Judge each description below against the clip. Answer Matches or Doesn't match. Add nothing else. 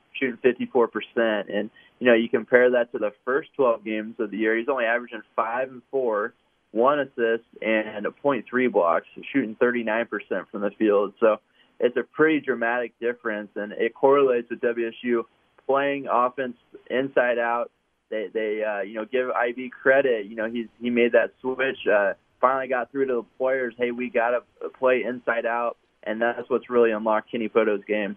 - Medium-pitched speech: Doesn't match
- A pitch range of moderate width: Doesn't match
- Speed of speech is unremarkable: Matches